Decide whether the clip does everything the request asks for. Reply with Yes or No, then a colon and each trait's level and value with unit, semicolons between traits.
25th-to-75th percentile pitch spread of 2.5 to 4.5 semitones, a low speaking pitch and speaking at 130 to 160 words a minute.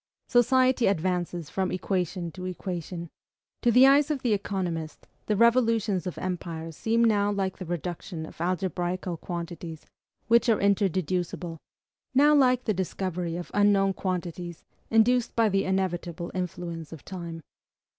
No: average, 3.8 semitones; medium, 185 Hz; average, 140 wpm